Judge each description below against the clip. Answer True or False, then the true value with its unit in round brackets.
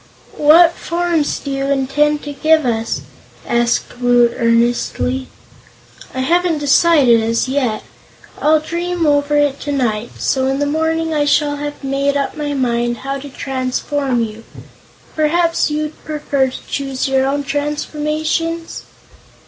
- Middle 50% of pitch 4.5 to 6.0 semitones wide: False (2.8 semitones)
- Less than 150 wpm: True (135 wpm)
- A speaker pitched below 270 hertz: False (285 Hz)